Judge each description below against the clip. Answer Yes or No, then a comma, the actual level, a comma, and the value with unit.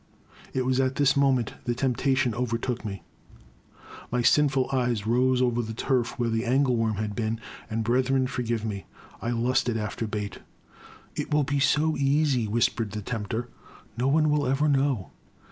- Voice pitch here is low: Yes, low, 125 Hz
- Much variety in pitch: No, average, 3.0 semitones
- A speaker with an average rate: Yes, average, 175 wpm